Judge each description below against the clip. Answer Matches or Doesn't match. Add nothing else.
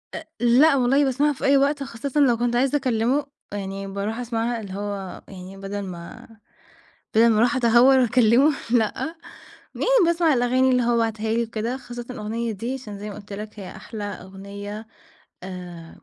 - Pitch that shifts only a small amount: Doesn't match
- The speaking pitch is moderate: Doesn't match